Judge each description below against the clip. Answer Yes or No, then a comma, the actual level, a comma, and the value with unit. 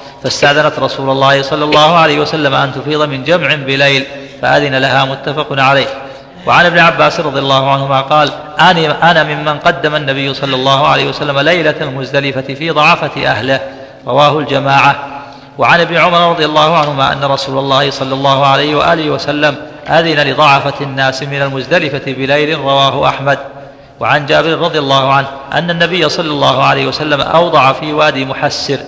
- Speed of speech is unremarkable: No, fast, 160 wpm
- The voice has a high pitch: No, medium, 140 Hz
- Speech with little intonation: Yes, narrow, 1.9 semitones